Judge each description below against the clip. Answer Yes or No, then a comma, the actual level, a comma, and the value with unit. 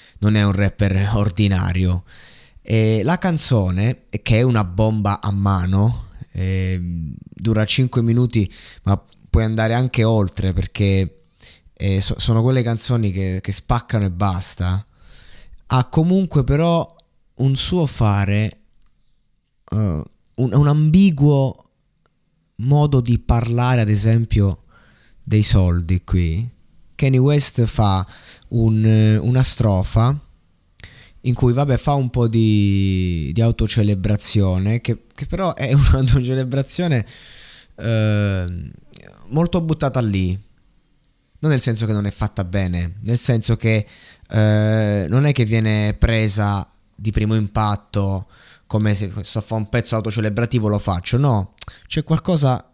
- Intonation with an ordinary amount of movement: Yes, average, 3.8 semitones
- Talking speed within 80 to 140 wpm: Yes, average, 125 wpm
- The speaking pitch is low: Yes, low, 110 Hz